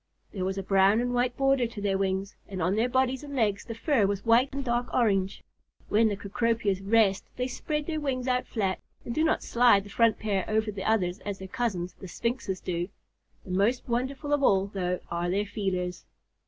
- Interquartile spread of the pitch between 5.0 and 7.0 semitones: No, average, 4.3 semitones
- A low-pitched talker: No, high, 215 Hz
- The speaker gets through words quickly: Yes, fast, 210 wpm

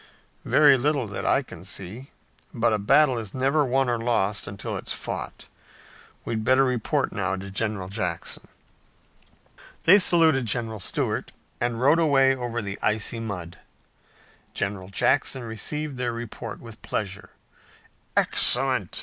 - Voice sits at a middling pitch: No, low, 115 Hz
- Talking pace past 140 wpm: No, slow, 135 wpm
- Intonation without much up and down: No, average, 4.5 semitones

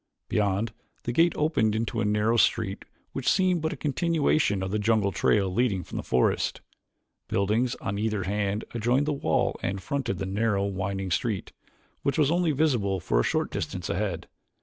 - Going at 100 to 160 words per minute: No, average, 175 wpm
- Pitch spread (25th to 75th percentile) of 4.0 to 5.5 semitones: Yes, average, 5.1 semitones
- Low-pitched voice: Yes, low, 105 Hz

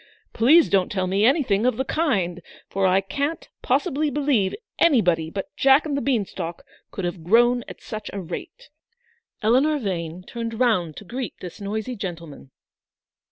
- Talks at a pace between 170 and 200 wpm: No, average, 160 wpm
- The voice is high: Yes, high, 215 Hz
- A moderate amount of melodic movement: No, wide, 6.2 semitones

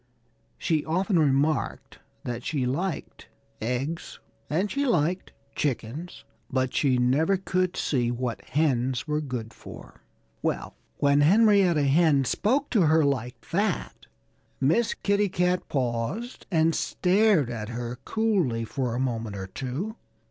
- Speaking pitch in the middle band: Yes, medium, 150 Hz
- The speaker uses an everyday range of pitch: No, wide, 6.6 semitones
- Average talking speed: No, slow, 130 wpm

